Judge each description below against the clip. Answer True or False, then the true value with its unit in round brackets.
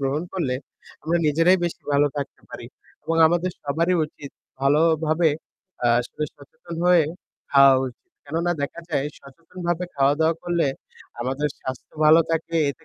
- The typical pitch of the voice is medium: True (160 Hz)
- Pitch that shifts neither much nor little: True (3.2 semitones)